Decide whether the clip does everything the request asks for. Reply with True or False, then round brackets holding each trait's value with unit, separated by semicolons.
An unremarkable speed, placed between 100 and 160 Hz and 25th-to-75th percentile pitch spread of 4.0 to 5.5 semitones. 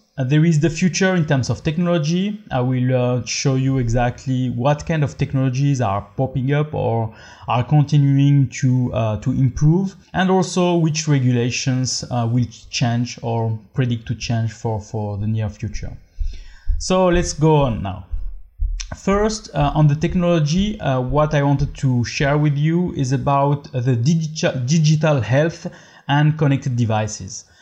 True (155 wpm; 135 Hz; 4.7 semitones)